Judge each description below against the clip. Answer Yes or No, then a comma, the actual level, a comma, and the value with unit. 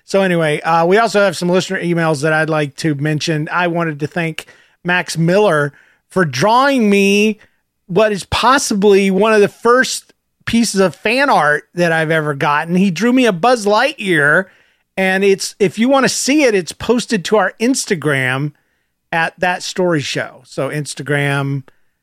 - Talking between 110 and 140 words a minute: No, average, 170 wpm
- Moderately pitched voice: Yes, medium, 180 Hz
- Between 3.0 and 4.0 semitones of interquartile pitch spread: No, wide, 5.4 semitones